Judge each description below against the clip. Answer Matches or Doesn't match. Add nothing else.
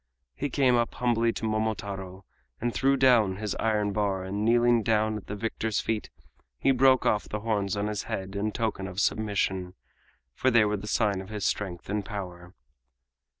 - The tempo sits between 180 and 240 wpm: Matches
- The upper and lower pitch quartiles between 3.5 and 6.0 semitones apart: Doesn't match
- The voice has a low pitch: Matches